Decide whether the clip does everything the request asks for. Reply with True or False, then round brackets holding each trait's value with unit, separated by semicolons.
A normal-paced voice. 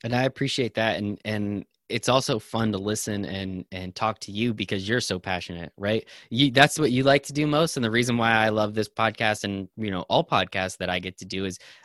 False (245 wpm)